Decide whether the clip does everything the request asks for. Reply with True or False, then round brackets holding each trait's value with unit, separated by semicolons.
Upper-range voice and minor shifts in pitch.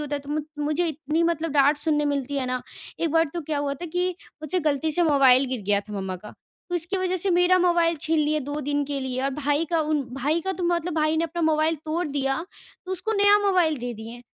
False (305 Hz; 3.4 semitones)